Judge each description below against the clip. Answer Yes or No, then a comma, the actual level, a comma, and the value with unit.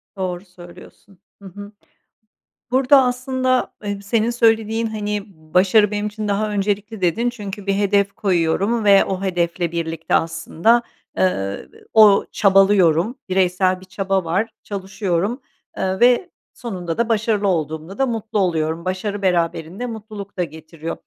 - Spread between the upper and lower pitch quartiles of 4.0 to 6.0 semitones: No, average, 3.5 semitones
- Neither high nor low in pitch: No, high, 200 Hz